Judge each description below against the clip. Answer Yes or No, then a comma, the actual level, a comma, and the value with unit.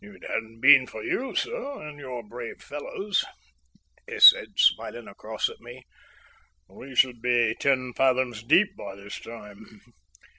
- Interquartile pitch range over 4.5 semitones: No, average, 3.9 semitones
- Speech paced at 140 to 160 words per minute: Yes, average, 150 wpm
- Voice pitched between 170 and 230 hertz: No, low, 125 Hz